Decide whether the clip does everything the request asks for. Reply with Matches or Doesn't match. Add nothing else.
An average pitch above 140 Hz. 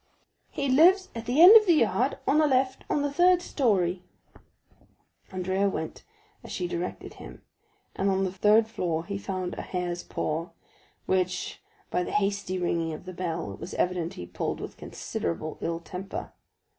Matches